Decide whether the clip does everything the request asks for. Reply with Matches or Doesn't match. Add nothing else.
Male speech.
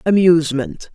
Doesn't match